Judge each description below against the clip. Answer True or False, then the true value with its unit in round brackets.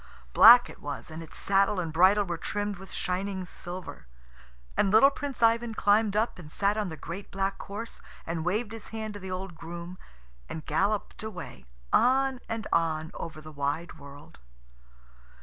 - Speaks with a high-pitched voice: True (195 Hz)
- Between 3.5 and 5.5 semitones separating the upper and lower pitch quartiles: True (4.5 semitones)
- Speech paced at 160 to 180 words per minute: True (170 wpm)